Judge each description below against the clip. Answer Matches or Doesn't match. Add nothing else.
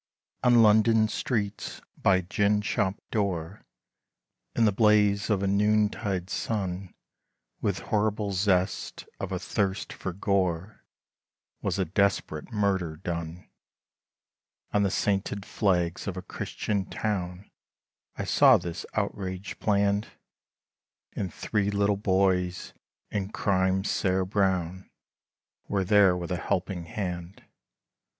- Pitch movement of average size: Doesn't match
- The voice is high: Doesn't match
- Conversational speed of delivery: Doesn't match